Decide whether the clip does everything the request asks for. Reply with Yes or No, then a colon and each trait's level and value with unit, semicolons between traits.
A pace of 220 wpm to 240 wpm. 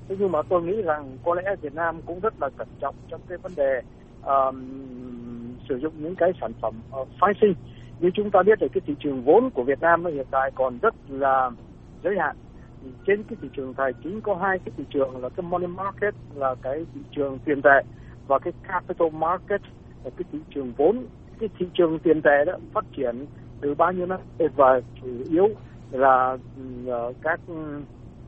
No: average, 205 wpm